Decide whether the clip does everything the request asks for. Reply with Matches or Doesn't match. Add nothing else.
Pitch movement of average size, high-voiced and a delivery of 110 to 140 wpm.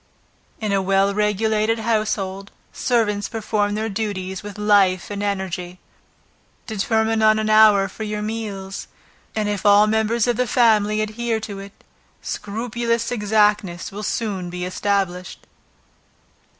Doesn't match